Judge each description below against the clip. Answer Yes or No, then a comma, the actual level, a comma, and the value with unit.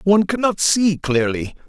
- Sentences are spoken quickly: No, average, 145 wpm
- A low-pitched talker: No, medium, 170 Hz